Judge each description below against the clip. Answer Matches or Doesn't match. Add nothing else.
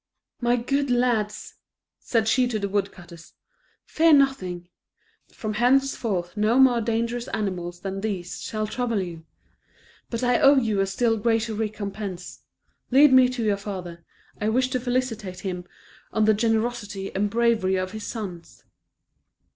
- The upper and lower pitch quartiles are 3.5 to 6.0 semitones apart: Matches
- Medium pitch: Doesn't match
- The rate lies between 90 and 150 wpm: Matches